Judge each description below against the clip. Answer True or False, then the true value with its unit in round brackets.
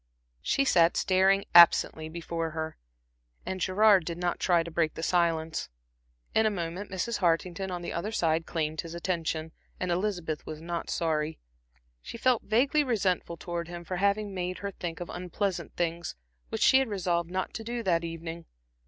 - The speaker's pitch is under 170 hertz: False (175 Hz)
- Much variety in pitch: False (2.8 semitones)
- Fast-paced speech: False (175 wpm)